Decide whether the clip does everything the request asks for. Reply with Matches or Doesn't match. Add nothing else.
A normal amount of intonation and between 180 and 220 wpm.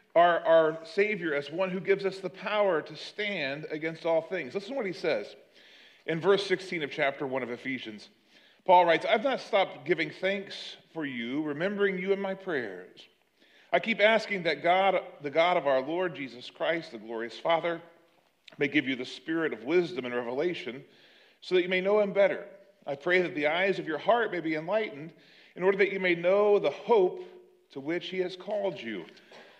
Matches